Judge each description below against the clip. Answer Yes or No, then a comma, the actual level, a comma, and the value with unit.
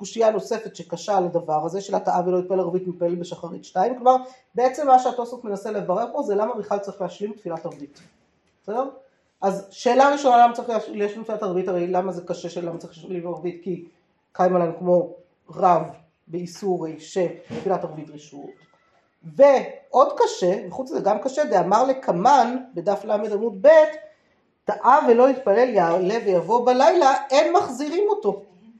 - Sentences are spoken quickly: Yes, fast, 160 wpm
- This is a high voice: Yes, high, 195 Hz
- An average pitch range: No, wide, 5.9 semitones